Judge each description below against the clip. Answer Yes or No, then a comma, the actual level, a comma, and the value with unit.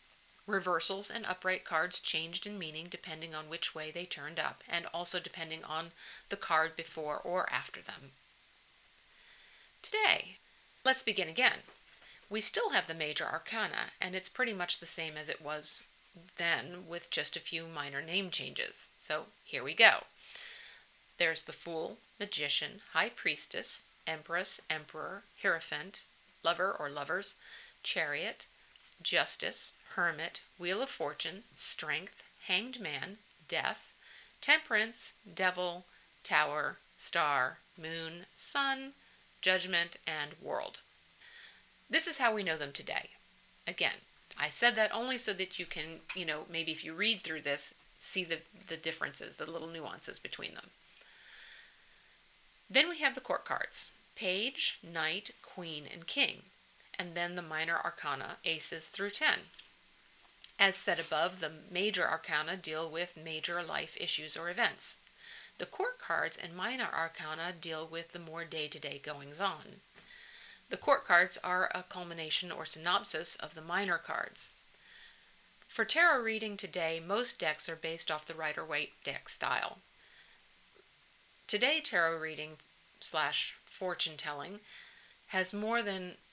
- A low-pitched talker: No, medium, 175 Hz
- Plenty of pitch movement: No, average, 4.1 semitones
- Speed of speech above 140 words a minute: No, slow, 135 wpm